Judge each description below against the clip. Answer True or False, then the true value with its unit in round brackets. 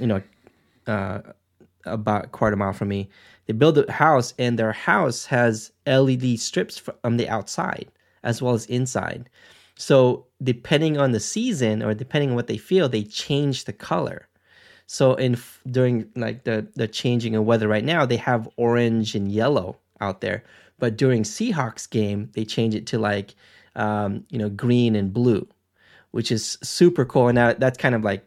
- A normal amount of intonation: True (3.0 semitones)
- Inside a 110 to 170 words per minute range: False (180 wpm)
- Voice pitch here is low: True (120 Hz)